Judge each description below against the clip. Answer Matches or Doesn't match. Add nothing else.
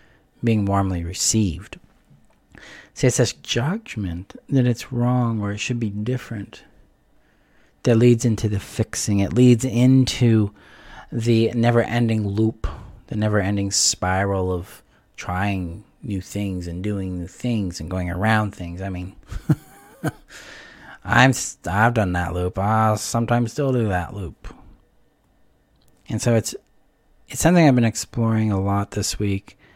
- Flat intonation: Doesn't match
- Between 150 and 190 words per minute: Doesn't match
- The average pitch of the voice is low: Matches